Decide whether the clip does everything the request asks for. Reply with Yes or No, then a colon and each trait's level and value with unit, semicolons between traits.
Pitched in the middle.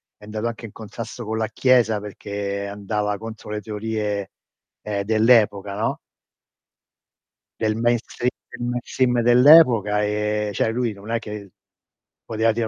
No: low, 110 Hz